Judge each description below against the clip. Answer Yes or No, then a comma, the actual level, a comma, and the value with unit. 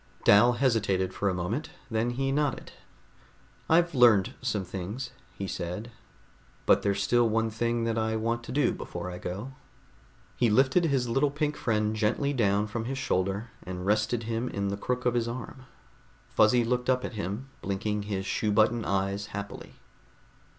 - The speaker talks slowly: No, average, 170 wpm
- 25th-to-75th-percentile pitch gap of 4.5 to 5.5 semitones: No, average, 3.7 semitones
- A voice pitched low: Yes, low, 110 Hz